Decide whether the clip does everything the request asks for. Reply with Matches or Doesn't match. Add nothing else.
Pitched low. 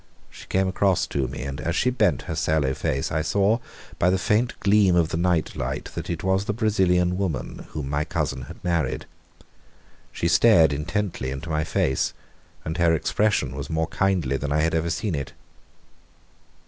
Matches